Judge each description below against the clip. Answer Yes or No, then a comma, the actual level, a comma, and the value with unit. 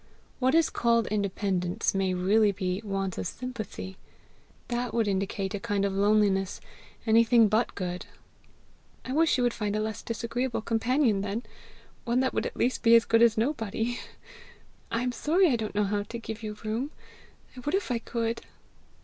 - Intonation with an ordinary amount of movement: Yes, average, 3.2 semitones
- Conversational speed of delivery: Yes, average, 175 wpm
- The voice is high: Yes, high, 225 Hz